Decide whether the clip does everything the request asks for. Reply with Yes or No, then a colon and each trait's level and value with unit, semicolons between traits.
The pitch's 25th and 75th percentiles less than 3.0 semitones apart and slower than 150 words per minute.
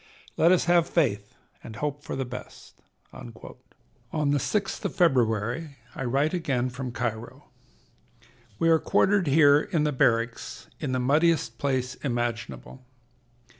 No: average, 4.8 semitones; slow, 135 wpm